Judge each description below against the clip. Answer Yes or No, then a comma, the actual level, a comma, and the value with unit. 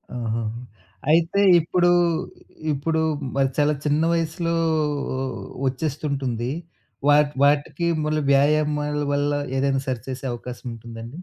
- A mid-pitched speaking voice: Yes, medium, 145 Hz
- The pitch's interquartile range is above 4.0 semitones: No, average, 2.9 semitones